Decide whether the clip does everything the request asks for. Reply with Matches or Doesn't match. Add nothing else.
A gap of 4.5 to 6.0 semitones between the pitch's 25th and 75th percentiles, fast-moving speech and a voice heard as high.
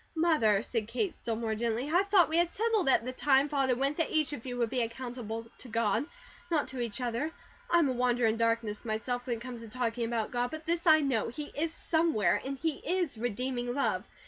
Matches